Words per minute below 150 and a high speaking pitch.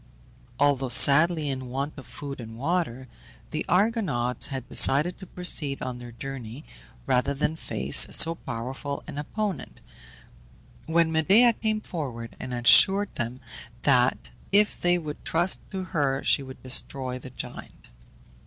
No: average, 140 wpm; medium, 140 Hz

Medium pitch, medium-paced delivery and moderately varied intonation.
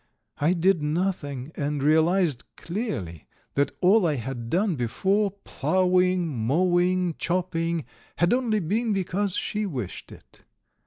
No: medium, 175 Hz; slow, 120 wpm; average, 4.6 semitones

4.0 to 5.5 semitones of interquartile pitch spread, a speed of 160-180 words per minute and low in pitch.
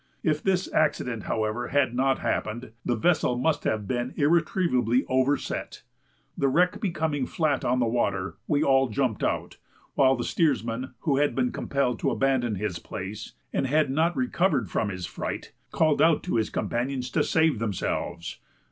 Yes: average, 4.8 semitones; average, 165 wpm; low, 130 Hz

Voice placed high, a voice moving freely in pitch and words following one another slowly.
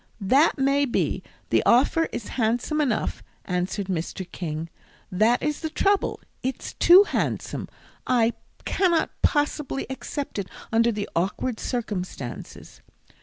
Yes: high, 240 Hz; wide, 6.7 semitones; slow, 120 wpm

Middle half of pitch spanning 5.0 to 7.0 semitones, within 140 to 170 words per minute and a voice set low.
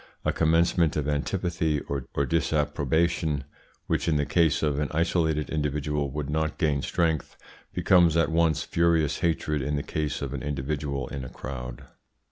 No: narrow, 2.4 semitones; average, 155 wpm; very low, 75 Hz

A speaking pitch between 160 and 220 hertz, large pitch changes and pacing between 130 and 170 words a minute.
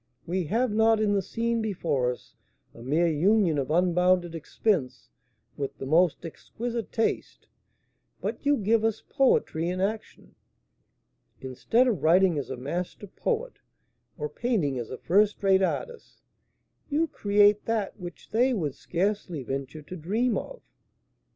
Yes: high, 190 Hz; wide, 5.9 semitones; average, 145 wpm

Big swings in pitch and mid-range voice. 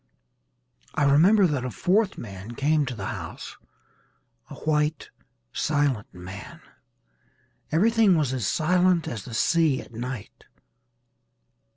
Yes: wide, 6.0 semitones; medium, 145 Hz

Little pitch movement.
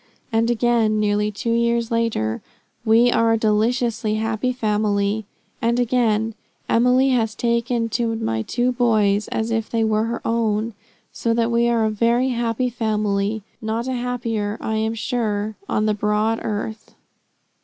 Yes: narrow, 1.7 semitones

